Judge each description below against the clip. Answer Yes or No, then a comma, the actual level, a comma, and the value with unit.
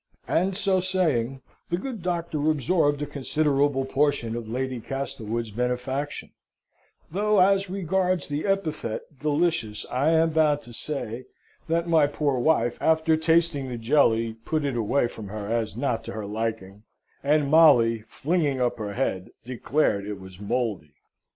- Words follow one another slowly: No, average, 150 wpm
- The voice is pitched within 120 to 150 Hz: Yes, medium, 140 Hz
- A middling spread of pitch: No, wide, 5.7 semitones